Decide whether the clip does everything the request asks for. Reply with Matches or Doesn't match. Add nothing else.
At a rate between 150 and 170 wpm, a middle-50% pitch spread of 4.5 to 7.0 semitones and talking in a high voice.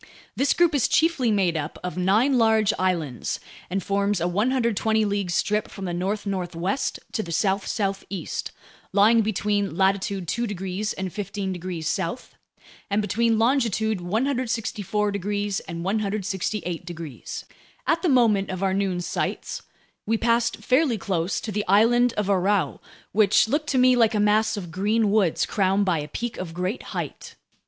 Doesn't match